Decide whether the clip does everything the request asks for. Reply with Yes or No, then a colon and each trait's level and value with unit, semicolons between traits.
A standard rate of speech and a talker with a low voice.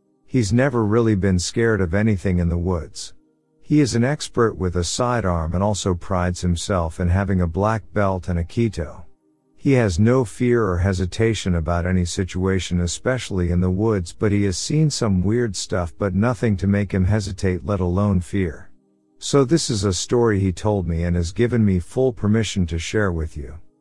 Yes: average, 190 wpm; low, 100 Hz